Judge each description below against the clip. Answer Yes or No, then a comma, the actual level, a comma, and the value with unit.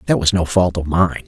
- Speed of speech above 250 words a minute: Yes, fast, 285 wpm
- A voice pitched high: No, very low, 90 Hz